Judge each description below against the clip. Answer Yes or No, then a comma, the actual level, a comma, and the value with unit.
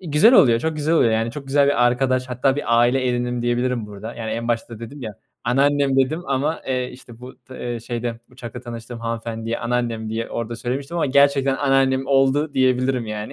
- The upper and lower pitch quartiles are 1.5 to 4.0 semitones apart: Yes, narrow, 2.5 semitones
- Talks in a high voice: No, low, 125 Hz